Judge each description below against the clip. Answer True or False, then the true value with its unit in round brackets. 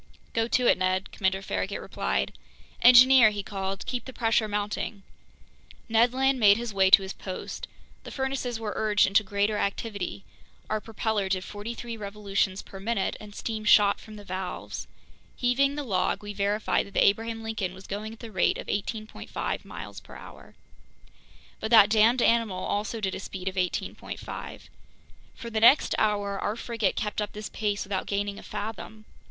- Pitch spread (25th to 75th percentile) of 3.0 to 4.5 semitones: False (2.4 semitones)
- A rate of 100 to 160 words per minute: False (175 wpm)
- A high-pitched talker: True (210 Hz)